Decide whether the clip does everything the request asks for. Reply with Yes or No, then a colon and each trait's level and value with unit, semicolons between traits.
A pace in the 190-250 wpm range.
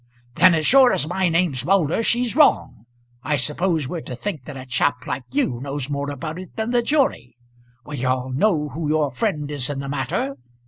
Yes: average, 200 wpm